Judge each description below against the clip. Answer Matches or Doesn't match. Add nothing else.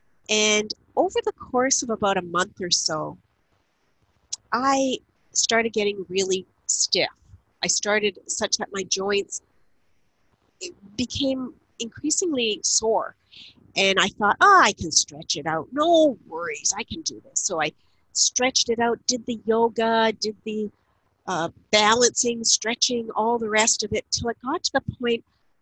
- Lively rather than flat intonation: Doesn't match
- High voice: Matches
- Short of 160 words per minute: Matches